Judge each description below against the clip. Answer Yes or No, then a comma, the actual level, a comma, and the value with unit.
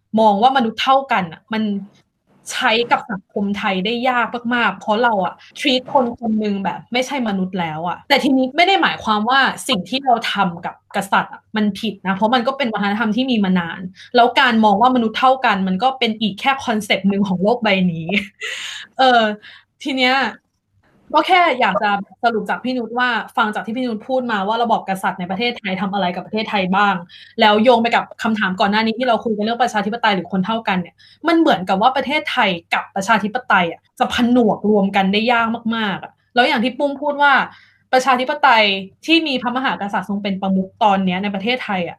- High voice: Yes, high, 220 Hz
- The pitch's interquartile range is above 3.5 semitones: Yes, average, 4.1 semitones